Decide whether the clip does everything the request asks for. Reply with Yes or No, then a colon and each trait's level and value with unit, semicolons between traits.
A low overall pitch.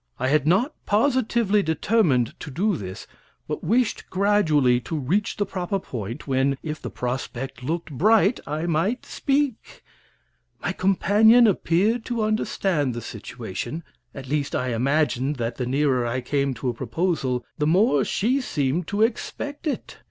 No: medium, 160 Hz